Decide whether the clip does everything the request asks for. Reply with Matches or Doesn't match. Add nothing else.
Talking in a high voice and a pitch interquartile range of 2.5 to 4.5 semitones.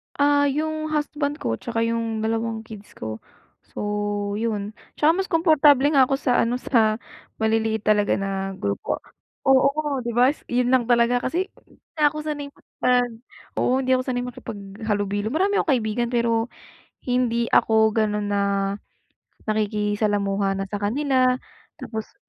Matches